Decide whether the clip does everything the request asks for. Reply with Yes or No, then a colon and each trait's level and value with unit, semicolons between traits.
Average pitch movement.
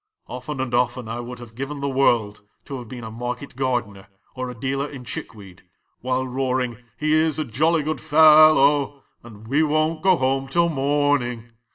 Yes: average, 3.4 semitones